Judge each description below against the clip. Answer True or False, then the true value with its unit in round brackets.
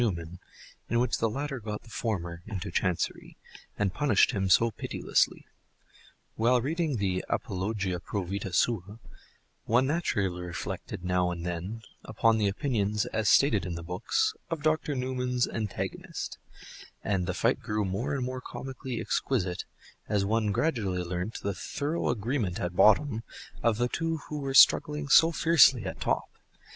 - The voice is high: False (110 Hz)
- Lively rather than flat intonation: True (5.7 semitones)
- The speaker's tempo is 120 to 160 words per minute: True (150 wpm)